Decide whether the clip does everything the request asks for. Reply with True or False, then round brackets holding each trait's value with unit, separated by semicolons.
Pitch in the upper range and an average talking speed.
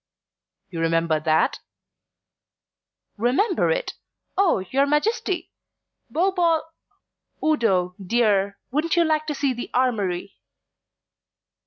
False (260 Hz; 105 wpm)